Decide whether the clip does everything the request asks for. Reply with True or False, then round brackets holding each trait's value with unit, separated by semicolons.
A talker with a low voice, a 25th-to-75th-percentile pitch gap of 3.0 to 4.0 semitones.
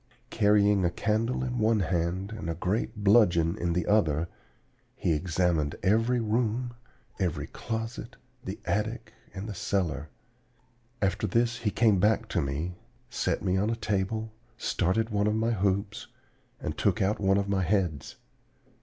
True (100 Hz; 3.7 semitones)